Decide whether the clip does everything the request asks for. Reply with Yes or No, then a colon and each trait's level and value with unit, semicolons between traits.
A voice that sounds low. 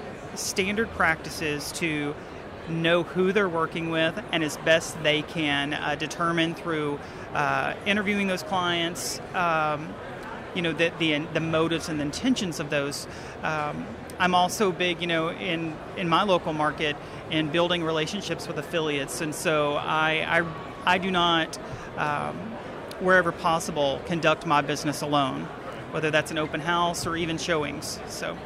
No: medium, 165 Hz